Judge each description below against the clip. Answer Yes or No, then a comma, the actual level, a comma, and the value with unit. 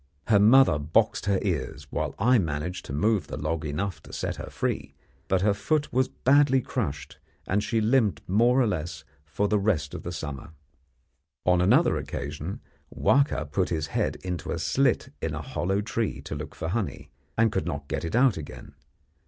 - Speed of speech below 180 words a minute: No, average, 185 wpm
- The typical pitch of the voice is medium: No, very low, 95 Hz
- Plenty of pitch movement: Yes, wide, 6.5 semitones